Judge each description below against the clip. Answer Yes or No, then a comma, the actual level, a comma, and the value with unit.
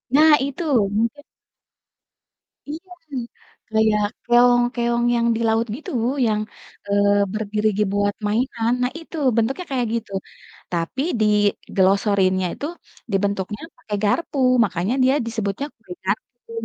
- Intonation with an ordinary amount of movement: Yes, average, 3.1 semitones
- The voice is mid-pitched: No, high, 220 Hz